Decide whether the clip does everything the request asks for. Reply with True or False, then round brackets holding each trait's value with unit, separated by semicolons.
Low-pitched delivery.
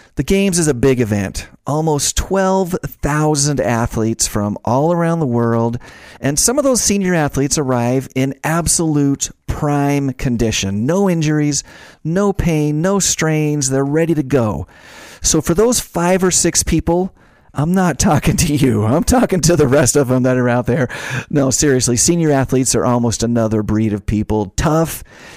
False (145 Hz)